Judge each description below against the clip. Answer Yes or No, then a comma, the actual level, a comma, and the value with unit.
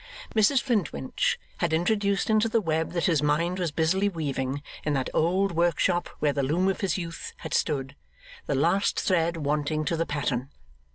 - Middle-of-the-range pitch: Yes, medium, 165 Hz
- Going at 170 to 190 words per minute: Yes, average, 175 wpm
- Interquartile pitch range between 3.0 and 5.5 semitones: Yes, average, 4.3 semitones